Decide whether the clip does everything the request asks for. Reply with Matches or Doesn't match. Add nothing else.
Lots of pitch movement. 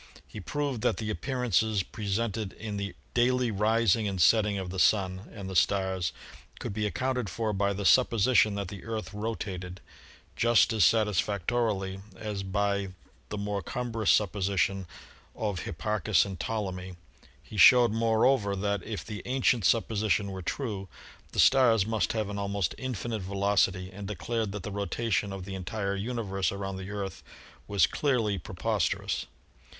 Doesn't match